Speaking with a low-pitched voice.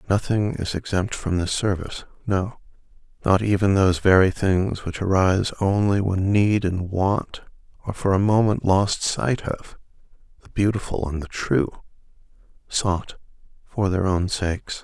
Yes: very low, 95 Hz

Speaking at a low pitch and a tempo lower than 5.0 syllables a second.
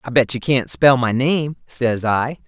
Yes: low, 130 Hz; 4.0 syllables/s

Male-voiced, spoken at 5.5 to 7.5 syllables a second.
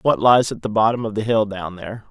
Yes: male; 5.9 syllables/s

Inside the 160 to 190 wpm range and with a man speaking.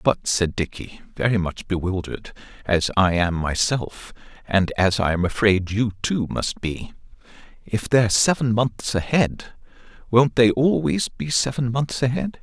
No: average, 150 wpm; male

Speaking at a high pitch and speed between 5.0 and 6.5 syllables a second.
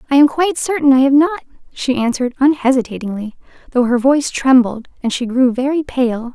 Yes: very high, 265 Hz; 5.9 syllables/s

